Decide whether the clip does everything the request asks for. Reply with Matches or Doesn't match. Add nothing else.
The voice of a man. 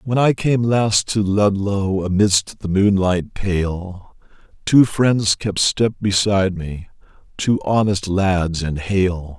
Matches